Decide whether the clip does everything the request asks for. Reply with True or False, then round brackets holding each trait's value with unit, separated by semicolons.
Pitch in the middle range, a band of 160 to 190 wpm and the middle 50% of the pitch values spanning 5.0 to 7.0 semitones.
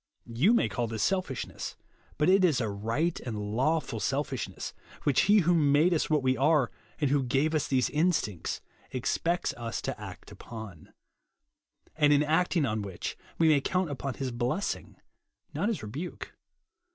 True (145 Hz; 165 wpm; 5.4 semitones)